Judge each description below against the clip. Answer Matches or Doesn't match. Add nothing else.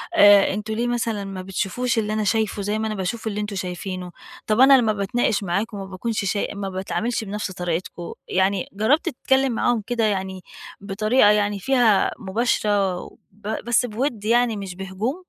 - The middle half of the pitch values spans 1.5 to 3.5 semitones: Matches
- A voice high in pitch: Matches